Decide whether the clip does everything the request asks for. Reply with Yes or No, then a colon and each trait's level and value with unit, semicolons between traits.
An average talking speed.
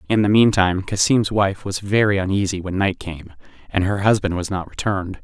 Yes: average, 195 wpm